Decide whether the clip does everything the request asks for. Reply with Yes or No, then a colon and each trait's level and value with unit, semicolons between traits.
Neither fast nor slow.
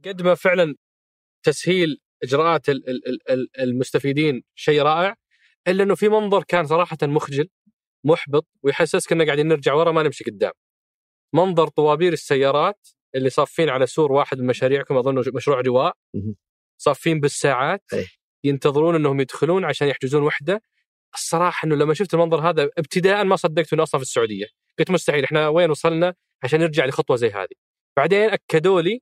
No: fast, 155 wpm